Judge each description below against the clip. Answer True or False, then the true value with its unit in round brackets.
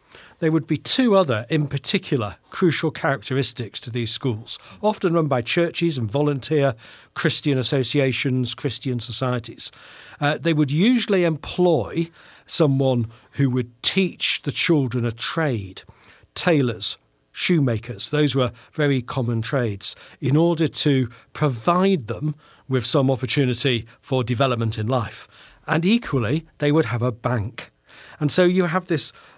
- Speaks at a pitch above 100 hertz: True (140 Hz)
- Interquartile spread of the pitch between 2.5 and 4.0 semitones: False (4.6 semitones)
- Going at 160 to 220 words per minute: False (135 wpm)